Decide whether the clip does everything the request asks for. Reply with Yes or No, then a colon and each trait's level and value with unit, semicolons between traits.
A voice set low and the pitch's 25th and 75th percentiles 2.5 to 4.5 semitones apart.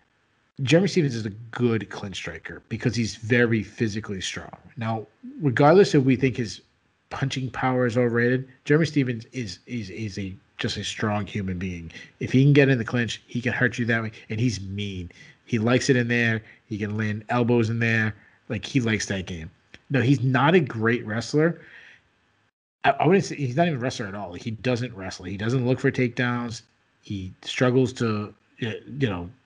Yes: low, 120 Hz; average, 3.8 semitones